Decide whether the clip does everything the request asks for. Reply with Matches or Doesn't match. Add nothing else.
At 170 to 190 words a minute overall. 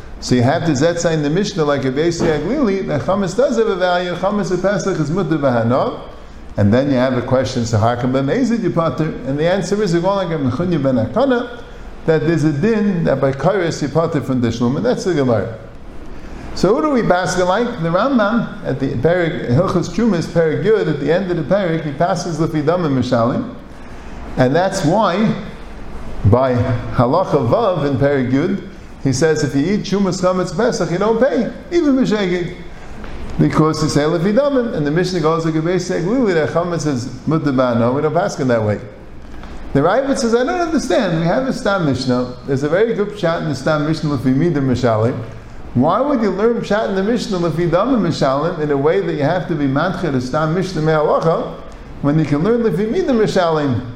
Matches